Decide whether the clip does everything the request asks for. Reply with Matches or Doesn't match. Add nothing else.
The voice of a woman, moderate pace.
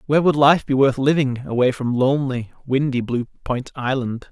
Doesn't match